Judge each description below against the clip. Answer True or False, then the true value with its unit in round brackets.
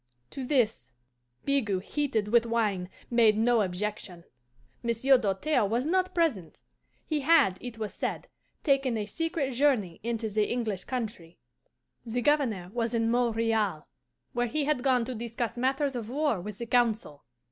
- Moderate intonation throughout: True (3.9 semitones)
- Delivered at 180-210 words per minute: False (150 wpm)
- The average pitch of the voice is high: True (235 Hz)